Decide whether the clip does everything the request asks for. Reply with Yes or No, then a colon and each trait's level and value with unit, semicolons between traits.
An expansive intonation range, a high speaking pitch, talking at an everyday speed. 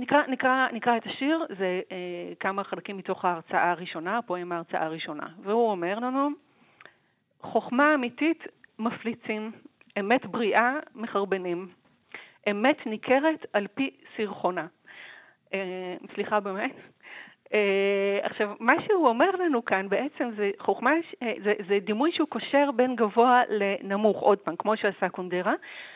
No: average, 4.8 semitones; high, 220 Hz; average, 130 wpm